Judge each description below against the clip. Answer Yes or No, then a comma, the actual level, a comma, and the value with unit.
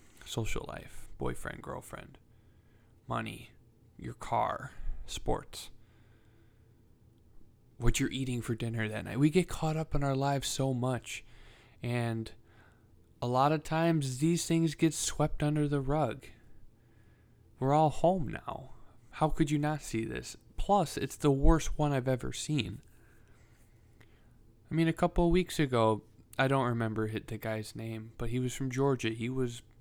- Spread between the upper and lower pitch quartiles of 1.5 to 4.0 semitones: No, average, 4.8 semitones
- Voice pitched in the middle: No, low, 120 Hz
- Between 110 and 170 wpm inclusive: Yes, average, 150 wpm